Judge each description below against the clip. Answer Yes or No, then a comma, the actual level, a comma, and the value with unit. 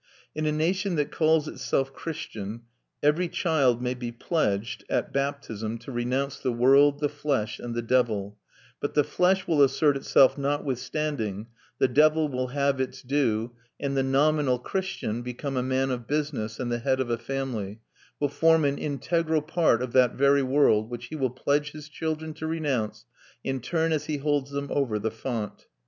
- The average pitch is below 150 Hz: Yes, low, 135 Hz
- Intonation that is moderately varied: Yes, average, 3.7 semitones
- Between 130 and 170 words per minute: No, average, 180 wpm